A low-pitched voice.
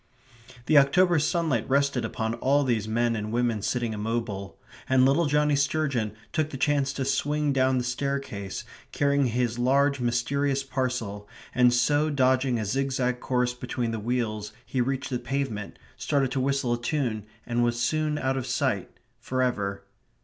Yes: low, 130 Hz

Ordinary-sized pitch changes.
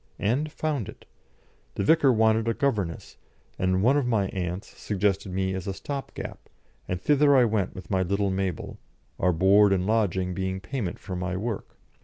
Yes: average, 3.7 semitones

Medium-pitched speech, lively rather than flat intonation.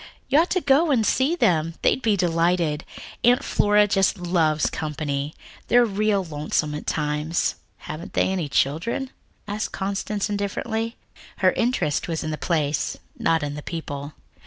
Yes: medium, 175 Hz; wide, 5.9 semitones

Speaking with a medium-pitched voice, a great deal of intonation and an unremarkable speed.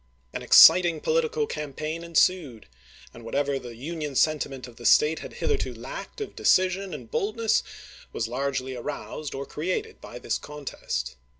Yes: medium, 150 Hz; wide, 5.7 semitones; average, 155 wpm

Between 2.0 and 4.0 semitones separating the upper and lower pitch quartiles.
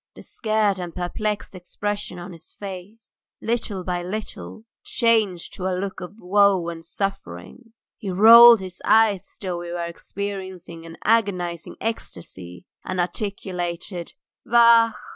Yes: average, 3.4 semitones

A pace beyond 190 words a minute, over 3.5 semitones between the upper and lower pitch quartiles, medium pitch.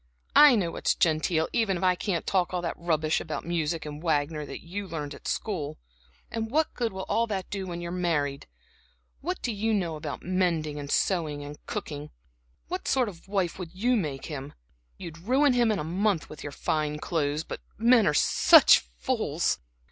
Yes: average, 200 wpm; average, 5.0 semitones; medium, 170 Hz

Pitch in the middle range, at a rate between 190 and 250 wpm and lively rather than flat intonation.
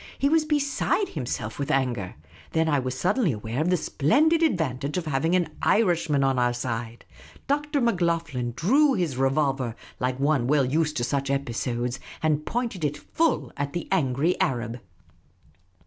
No: medium, 145 Hz; average, 165 wpm; wide, 6.1 semitones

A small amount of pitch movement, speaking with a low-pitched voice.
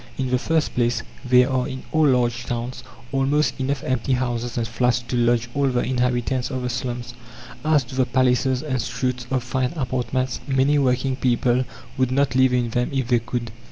Yes: narrow, 1.3 semitones; low, 125 Hz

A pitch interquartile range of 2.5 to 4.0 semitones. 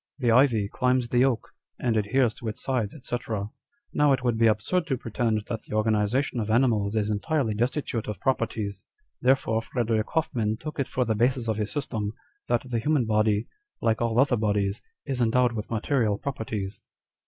Yes: average, 3.0 semitones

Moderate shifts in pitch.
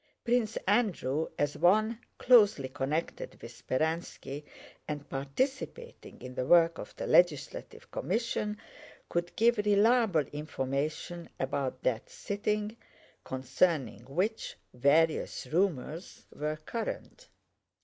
No: wide, 7.1 semitones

